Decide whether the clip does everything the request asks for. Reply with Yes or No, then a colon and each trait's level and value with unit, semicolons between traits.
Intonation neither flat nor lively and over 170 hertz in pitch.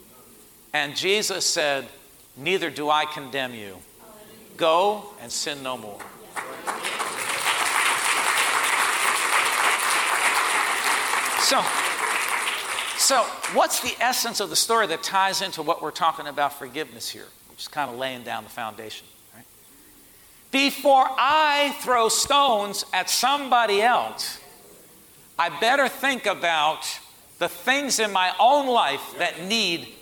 No: wide, 8.1 semitones; medium, 185 Hz